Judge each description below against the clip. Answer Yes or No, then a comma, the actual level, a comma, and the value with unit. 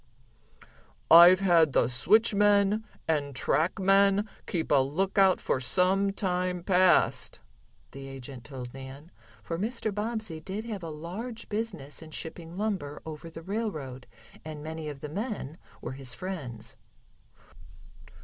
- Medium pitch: Yes, medium, 170 Hz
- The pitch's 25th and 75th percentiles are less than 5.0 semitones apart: No, average, 5.3 semitones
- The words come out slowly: Yes, slow, 125 wpm